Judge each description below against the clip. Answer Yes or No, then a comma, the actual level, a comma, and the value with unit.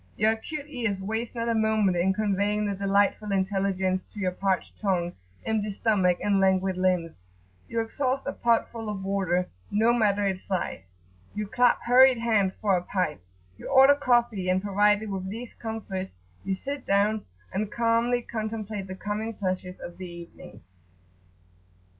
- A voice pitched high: Yes, high, 205 Hz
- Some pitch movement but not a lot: Yes, average, 3.0 semitones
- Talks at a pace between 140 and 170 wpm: Yes, average, 160 wpm